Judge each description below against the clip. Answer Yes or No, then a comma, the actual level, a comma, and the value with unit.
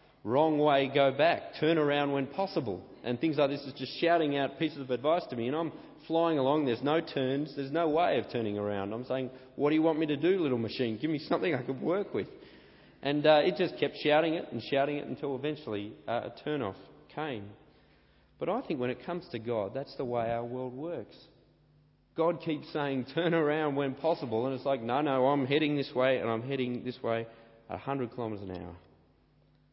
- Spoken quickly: Yes, fast, 220 wpm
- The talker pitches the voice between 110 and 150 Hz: Yes, medium, 140 Hz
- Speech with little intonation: No, average, 3.8 semitones